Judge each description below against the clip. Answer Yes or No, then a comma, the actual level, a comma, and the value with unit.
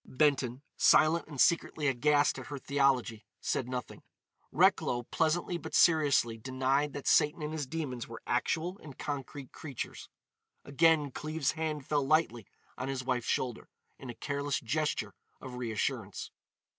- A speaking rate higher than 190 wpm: No, average, 145 wpm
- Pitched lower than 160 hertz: Yes, medium, 140 Hz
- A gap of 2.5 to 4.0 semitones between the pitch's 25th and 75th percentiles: Yes, average, 3.3 semitones